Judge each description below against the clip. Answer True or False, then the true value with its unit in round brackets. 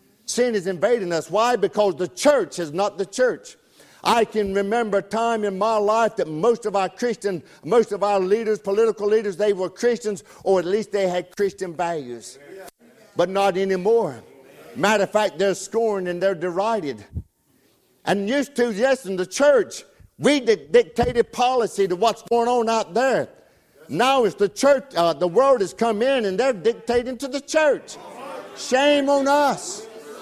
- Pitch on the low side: False (215 Hz)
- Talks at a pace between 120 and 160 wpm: False (175 wpm)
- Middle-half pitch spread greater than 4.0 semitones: False (3.7 semitones)